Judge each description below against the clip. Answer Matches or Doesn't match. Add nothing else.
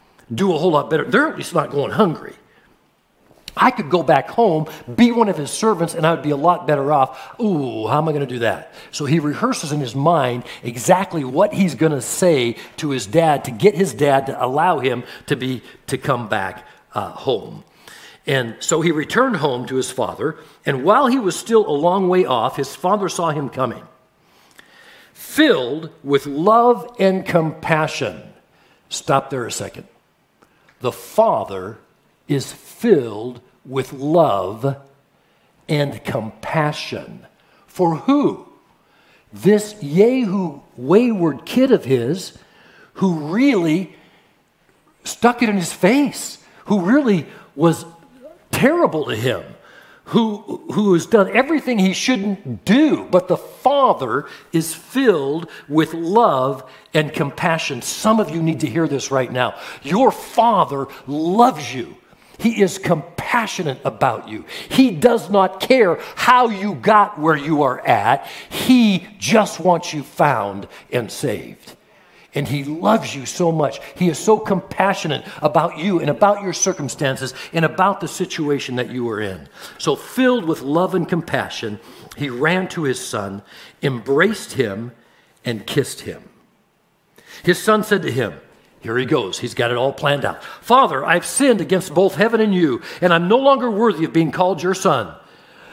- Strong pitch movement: Matches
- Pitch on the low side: Doesn't match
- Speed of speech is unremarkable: Matches